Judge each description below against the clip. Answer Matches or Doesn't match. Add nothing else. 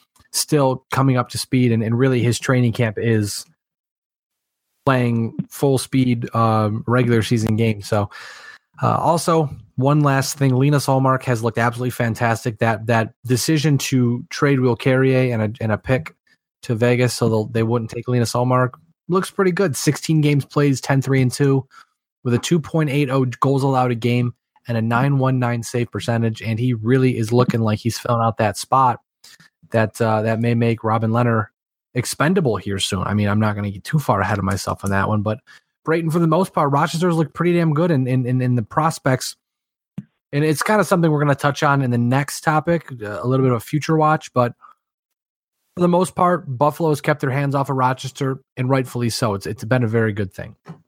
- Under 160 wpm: Doesn't match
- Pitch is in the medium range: Doesn't match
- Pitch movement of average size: Matches